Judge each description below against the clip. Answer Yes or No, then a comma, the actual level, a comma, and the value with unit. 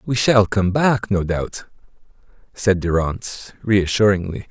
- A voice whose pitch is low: Yes, low, 100 Hz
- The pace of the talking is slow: Yes, slow, 120 wpm